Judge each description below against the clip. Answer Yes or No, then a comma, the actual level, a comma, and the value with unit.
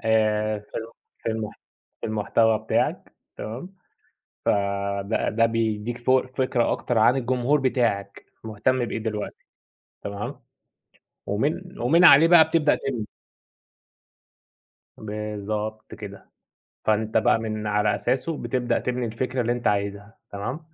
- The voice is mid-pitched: No, low, 110 Hz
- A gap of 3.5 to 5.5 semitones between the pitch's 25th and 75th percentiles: No, average, 3.1 semitones